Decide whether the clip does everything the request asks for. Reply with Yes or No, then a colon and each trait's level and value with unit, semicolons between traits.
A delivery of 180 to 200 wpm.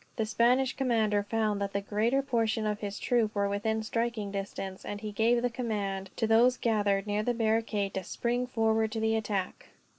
Yes: average, 190 wpm